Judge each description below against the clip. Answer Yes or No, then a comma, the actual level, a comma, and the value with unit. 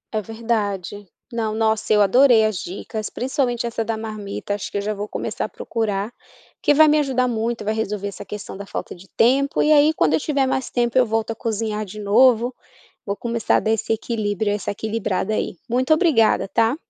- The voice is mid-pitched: No, high, 220 Hz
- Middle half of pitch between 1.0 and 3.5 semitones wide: Yes, average, 2.7 semitones